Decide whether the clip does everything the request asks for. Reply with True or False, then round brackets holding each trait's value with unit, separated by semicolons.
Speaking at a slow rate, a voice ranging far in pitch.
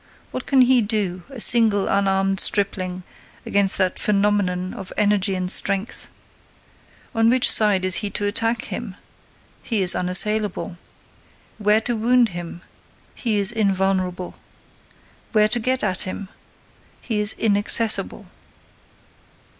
False (125 wpm; 2.9 semitones)